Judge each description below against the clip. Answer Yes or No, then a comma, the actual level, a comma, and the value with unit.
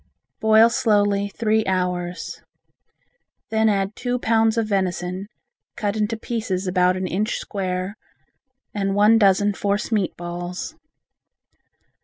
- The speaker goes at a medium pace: No, slow, 115 wpm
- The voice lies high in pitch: Yes, high, 200 Hz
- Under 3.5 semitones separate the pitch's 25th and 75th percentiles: Yes, average, 2.9 semitones